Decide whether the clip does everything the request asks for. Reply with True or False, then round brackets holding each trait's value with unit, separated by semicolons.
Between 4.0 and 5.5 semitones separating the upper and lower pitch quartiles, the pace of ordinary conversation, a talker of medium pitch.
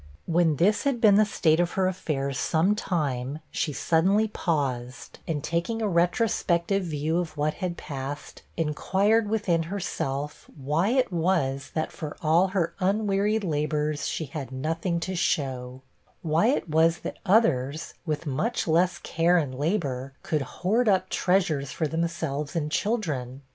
True (4.4 semitones; 150 wpm; 165 Hz)